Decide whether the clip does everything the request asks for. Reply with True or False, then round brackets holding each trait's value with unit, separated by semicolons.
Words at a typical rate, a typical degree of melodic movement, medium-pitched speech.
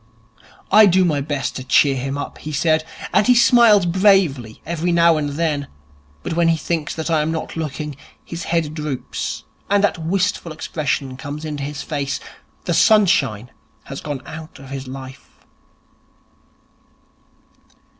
True (150 wpm; 3.4 semitones; 155 Hz)